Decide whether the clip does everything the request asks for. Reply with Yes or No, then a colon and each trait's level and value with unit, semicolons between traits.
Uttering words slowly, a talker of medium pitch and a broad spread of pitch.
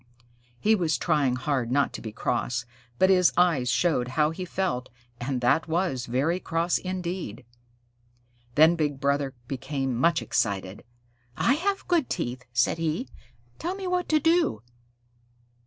No: average, 145 wpm; medium, 155 Hz; wide, 6.4 semitones